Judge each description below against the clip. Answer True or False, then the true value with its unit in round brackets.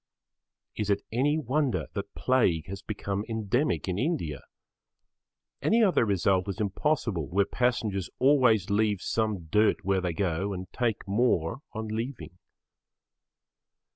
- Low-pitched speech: True (105 Hz)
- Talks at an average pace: False (130 wpm)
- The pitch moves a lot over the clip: False (4.3 semitones)